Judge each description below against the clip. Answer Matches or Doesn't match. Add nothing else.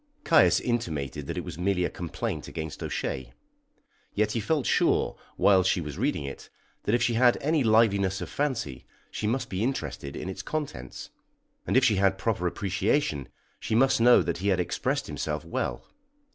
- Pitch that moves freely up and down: Matches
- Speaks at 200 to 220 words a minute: Doesn't match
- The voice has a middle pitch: Doesn't match